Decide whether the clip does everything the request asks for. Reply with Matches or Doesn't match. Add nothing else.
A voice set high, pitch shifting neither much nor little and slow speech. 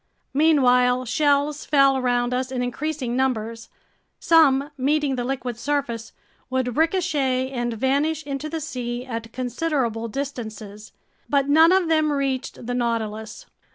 Matches